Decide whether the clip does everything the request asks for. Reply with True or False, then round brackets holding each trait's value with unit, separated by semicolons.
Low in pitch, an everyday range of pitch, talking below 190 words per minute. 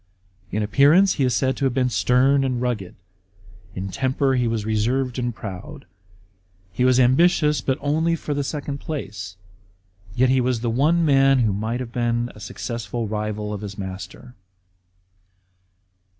True (125 Hz; 3.9 semitones; 160 wpm)